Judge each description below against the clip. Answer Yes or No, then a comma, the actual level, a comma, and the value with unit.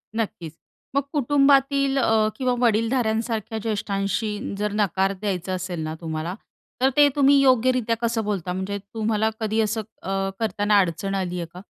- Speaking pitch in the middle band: No, high, 215 Hz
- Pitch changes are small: No, average, 3.5 semitones